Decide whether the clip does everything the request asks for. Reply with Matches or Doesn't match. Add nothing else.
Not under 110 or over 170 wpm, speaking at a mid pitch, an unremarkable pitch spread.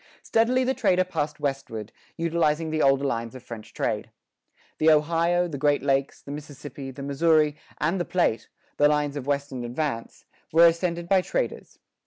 Matches